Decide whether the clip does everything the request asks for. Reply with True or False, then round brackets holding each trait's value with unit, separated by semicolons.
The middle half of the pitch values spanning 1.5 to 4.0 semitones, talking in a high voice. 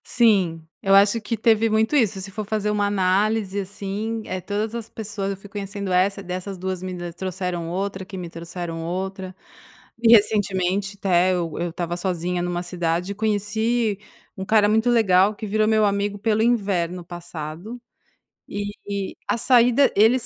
True (2.9 semitones; 200 Hz)